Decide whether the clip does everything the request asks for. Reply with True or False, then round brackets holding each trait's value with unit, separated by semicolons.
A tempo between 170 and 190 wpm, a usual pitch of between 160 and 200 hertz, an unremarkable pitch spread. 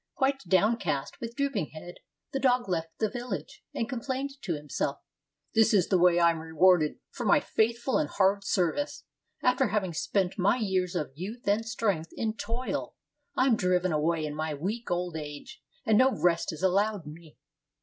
False (180 wpm; 190 Hz; 5.7 semitones)